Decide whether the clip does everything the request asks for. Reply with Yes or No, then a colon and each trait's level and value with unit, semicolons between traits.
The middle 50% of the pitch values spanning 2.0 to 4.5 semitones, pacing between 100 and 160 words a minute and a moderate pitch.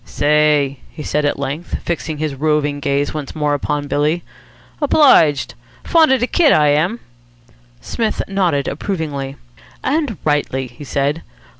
Yes: average, 3.4 semitones; average, 140 wpm; medium, 150 Hz